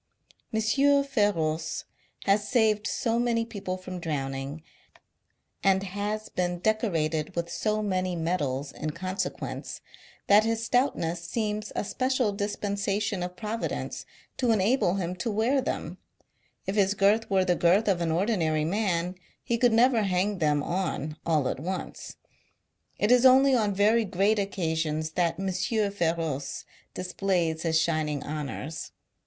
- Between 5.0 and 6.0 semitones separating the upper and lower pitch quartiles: No, average, 4.5 semitones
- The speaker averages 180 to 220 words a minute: No, slow, 135 wpm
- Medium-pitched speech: No, high, 195 Hz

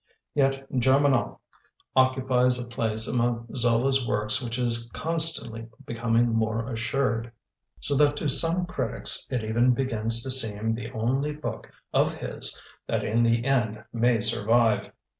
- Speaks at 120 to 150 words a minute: Yes, average, 140 wpm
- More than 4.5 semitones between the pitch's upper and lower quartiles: No, narrow, 2.6 semitones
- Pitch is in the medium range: No, low, 120 Hz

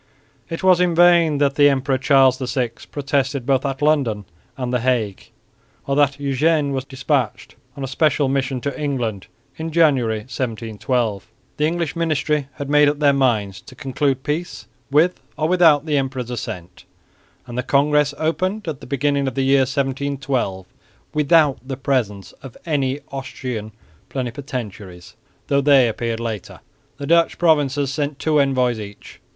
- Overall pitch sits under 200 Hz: Yes, low, 135 Hz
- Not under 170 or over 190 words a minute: No, average, 155 wpm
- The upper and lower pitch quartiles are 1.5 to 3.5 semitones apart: Yes, average, 2.8 semitones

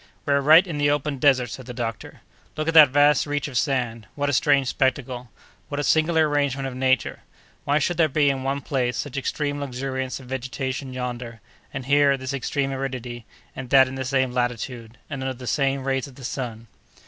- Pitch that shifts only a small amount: Yes, narrow, 2.2 semitones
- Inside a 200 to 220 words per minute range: Yes, fast, 205 wpm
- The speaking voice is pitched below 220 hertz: Yes, low, 135 Hz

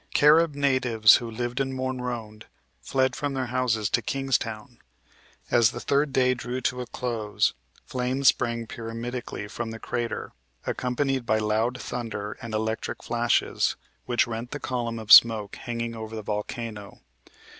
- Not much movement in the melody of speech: Yes, narrow, 2.3 semitones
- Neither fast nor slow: Yes, average, 150 wpm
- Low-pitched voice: Yes, low, 120 Hz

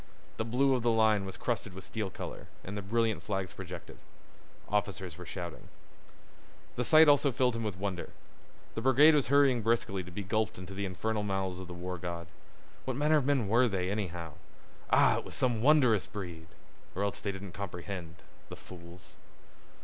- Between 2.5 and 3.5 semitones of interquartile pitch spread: No, average, 4.4 semitones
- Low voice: Yes, low, 100 Hz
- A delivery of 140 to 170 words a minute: No, average, 180 wpm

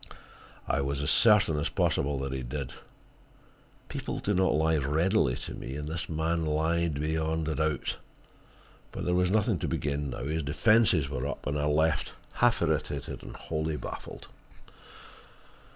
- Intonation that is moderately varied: No, narrow, 2.3 semitones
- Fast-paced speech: No, average, 165 wpm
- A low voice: Yes, very low, 75 Hz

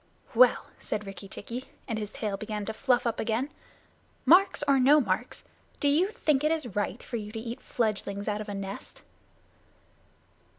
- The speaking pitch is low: No, high, 225 Hz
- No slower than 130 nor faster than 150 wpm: No, average, 175 wpm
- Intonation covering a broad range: No, average, 5.0 semitones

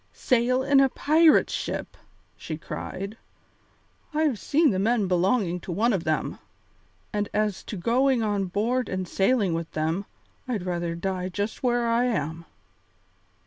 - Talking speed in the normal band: Yes, average, 145 wpm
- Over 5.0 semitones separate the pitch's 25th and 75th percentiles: Yes, wide, 5.4 semitones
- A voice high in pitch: Yes, high, 205 Hz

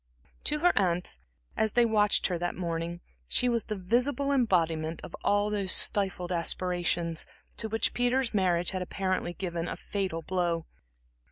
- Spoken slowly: No, average, 155 wpm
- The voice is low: No, medium, 185 Hz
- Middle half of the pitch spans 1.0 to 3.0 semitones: No, average, 4.1 semitones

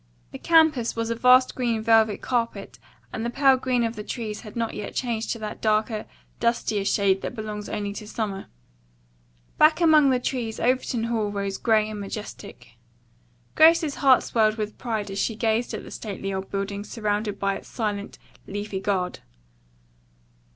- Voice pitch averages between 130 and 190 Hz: No, high, 220 Hz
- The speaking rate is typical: Yes, average, 170 wpm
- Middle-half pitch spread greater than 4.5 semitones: No, average, 2.7 semitones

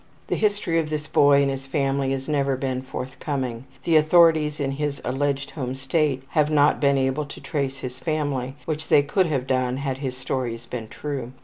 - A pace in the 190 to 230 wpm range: Yes, average, 195 wpm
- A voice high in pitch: No, medium, 140 Hz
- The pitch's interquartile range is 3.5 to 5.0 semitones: No, narrow, 2.4 semitones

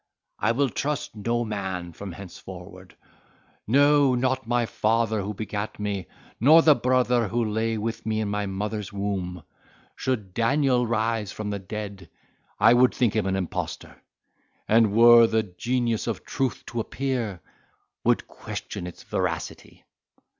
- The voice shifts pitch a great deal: No, average, 3.2 semitones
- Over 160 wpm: No, average, 140 wpm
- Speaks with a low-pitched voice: Yes, low, 110 Hz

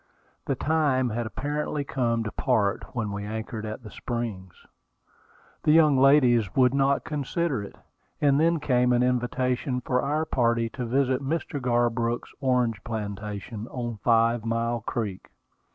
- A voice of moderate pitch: No, low, 125 Hz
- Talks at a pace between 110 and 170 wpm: Yes, average, 145 wpm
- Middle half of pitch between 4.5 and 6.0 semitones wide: No, average, 3.2 semitones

